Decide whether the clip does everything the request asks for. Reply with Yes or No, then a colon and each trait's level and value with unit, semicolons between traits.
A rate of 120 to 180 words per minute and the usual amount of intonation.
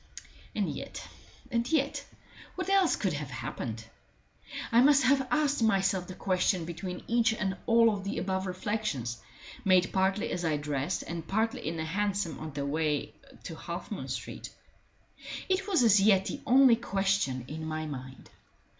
No: average, 165 wpm; wide, 6.4 semitones